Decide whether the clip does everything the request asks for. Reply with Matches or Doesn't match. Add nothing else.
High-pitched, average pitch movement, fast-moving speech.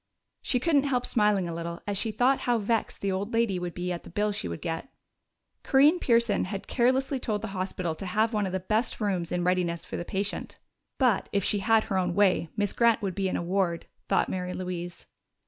Matches